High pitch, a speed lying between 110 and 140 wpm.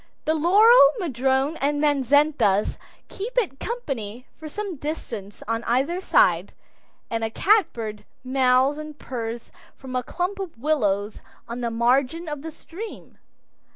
Yes: very high, 275 Hz; slow, 135 wpm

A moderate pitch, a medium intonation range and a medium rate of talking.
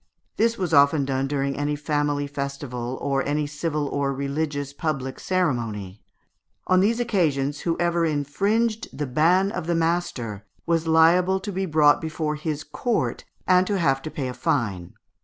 Yes: medium, 150 Hz; average, 3.8 semitones; average, 160 wpm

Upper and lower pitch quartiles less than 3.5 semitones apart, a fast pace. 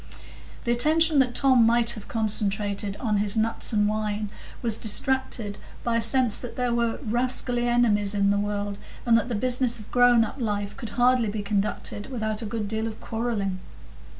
No: average, 2.8 semitones; average, 180 wpm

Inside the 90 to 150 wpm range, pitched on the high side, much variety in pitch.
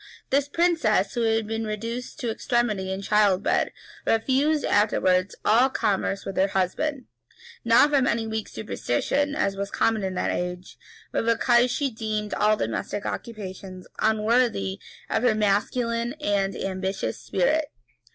No: average, 140 wpm; high, 220 Hz; average, 3.6 semitones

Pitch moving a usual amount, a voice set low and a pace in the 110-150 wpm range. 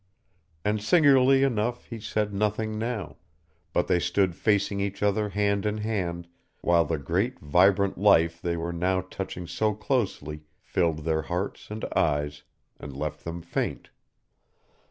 Yes: average, 4.1 semitones; low, 100 Hz; average, 145 wpm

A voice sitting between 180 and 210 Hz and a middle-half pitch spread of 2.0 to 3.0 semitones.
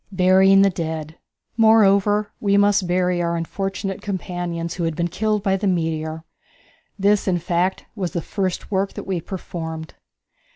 Yes: medium, 185 Hz; average, 2.7 semitones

